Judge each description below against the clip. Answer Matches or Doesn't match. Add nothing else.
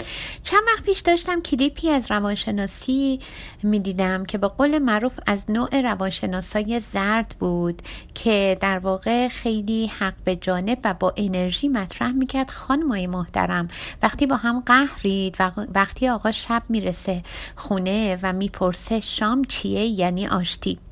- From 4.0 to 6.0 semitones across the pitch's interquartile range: Matches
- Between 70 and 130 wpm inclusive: Doesn't match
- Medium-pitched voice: Doesn't match